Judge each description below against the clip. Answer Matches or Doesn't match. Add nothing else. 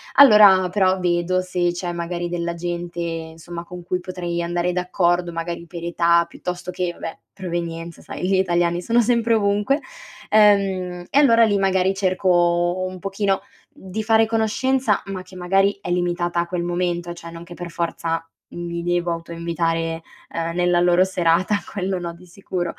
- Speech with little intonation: Matches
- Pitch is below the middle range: Doesn't match